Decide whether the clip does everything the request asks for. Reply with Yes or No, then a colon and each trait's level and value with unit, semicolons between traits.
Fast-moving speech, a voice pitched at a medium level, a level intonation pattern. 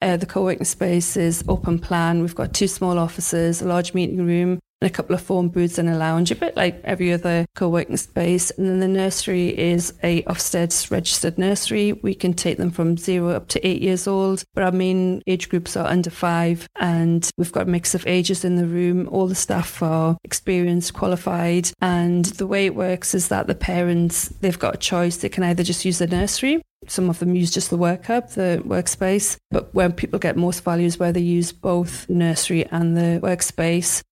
Yes: fast, 210 wpm; medium, 175 Hz; narrow, 1.3 semitones